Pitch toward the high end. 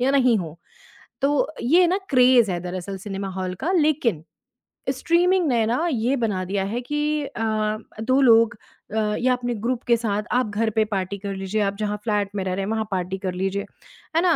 Yes: high, 225 Hz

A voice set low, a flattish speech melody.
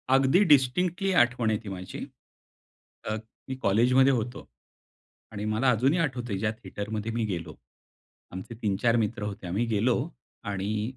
No: low, 110 Hz; average, 3.5 semitones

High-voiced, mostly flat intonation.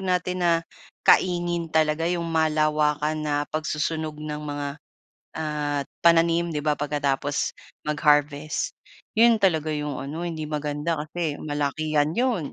No: medium, 155 Hz; narrow, 2.2 semitones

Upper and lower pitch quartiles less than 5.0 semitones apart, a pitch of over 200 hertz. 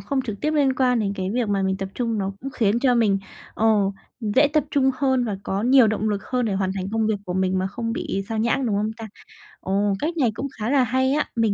Yes: average, 4.5 semitones; high, 225 Hz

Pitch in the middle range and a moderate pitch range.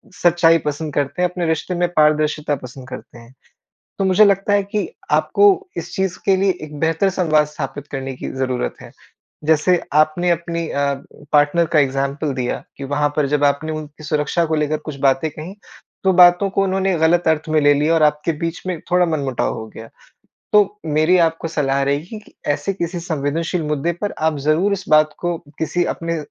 Yes: medium, 155 Hz; average, 3.2 semitones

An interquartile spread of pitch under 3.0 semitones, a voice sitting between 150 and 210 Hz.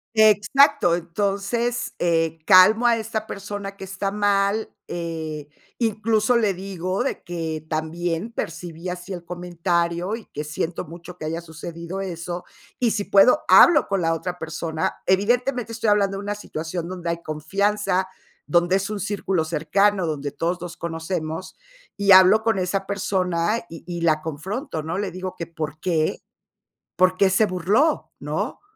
No: average, 3.5 semitones; medium, 185 Hz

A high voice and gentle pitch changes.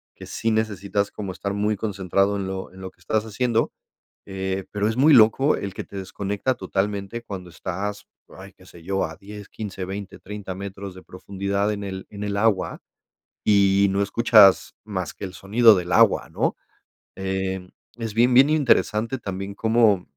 No: low, 100 Hz; narrow, 2.1 semitones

